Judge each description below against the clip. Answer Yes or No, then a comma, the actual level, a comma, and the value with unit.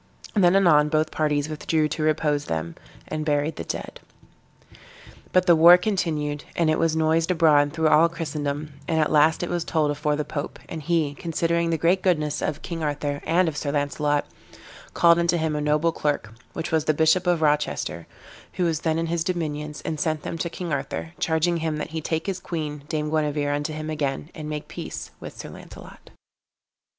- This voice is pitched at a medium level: Yes, medium, 155 Hz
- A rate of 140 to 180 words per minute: No, average, 195 wpm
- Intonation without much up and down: Yes, narrow, 2.0 semitones